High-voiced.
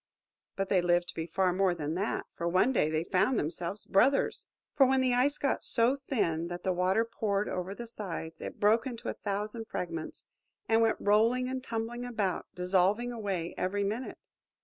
Yes: high, 205 Hz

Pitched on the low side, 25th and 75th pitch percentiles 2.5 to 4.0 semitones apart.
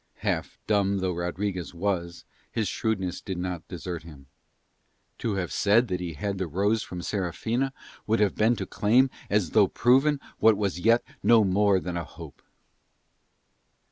Yes: low, 100 Hz; average, 3.7 semitones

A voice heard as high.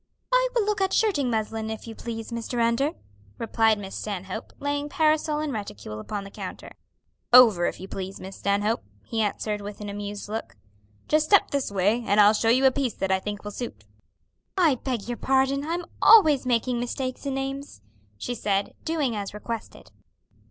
Yes: high, 230 Hz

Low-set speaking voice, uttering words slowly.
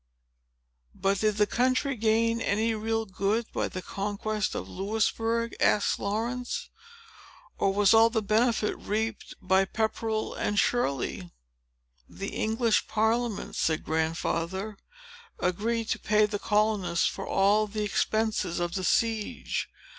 No: high, 215 Hz; slow, 125 wpm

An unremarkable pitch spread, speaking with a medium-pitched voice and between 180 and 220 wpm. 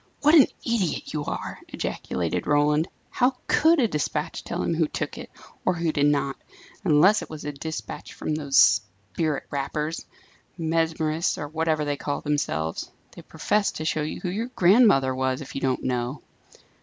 No: average, 3.2 semitones; medium, 155 Hz; average, 170 wpm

